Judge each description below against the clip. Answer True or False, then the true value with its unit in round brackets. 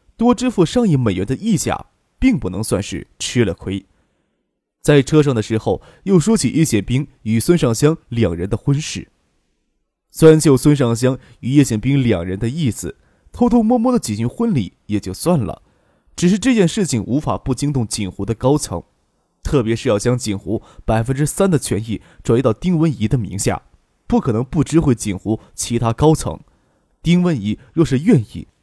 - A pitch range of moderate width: False (7.0 semitones)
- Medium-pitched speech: False (125 Hz)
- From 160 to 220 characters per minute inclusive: False (260 characters per minute)